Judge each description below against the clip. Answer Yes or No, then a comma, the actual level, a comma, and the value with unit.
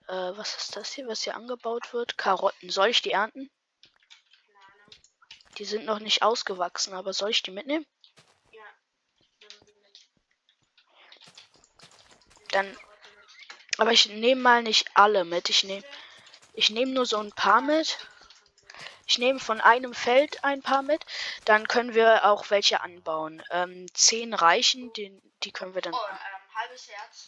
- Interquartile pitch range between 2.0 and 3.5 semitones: No, average, 4.3 semitones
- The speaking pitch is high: Yes, high, 220 Hz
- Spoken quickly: No, average, 145 wpm